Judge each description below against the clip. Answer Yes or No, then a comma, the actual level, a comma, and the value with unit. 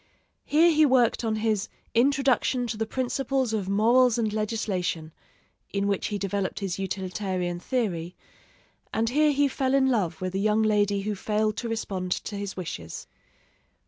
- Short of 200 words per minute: Yes, average, 160 wpm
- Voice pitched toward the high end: Yes, high, 215 Hz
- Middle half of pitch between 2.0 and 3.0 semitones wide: No, average, 4.1 semitones